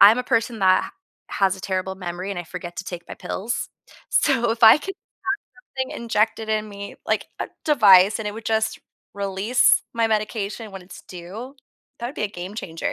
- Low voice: No, high, 210 Hz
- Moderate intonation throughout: Yes, average, 3.3 semitones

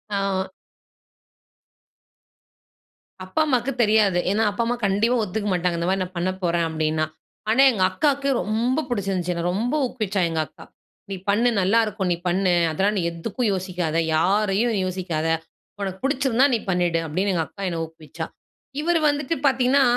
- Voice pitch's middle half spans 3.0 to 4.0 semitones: No, average, 4.8 semitones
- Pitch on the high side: Yes, high, 195 Hz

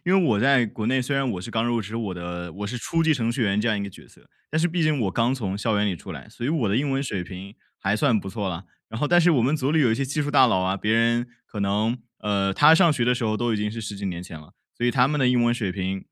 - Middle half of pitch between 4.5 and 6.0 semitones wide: Yes, average, 5.1 semitones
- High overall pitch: No, low, 115 Hz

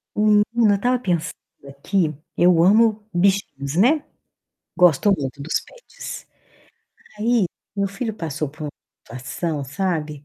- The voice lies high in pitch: No, medium, 180 Hz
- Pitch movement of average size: No, wide, 5.7 semitones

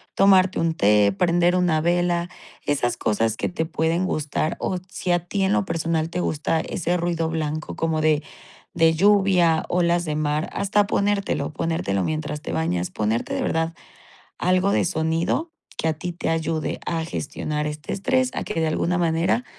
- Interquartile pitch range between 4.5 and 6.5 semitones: No, narrow, 2.4 semitones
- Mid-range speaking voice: Yes, medium, 165 Hz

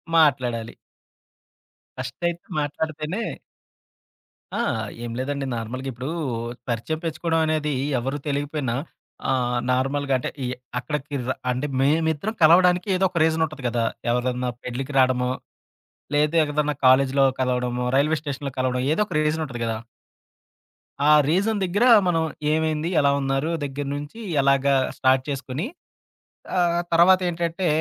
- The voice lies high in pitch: No, medium, 145 Hz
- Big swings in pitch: No, average, 3.7 semitones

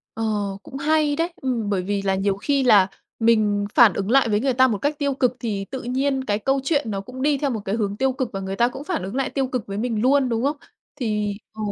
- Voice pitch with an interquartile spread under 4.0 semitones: No, average, 4.8 semitones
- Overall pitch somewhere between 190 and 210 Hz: No, high, 245 Hz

